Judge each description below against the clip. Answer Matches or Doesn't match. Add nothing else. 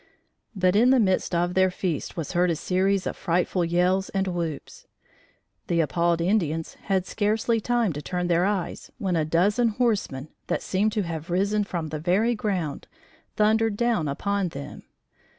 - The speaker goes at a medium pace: Matches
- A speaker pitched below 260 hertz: Matches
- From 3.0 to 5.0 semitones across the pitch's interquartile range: Matches